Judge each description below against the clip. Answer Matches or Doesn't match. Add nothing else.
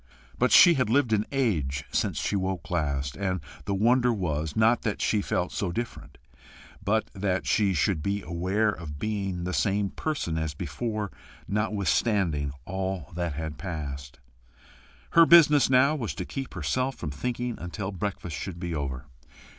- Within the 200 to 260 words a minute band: Doesn't match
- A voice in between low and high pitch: Doesn't match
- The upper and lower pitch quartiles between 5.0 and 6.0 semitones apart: Matches